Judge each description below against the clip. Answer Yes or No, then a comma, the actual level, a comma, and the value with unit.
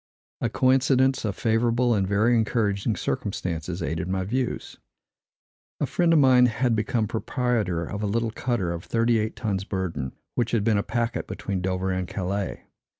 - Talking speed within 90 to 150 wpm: No, average, 165 wpm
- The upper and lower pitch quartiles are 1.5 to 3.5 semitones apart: No, average, 4.2 semitones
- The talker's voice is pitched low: Yes, low, 110 Hz